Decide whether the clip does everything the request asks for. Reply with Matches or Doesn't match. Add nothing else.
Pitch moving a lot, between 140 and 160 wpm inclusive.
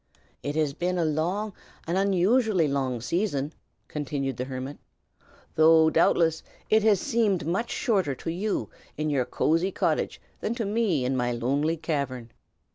Matches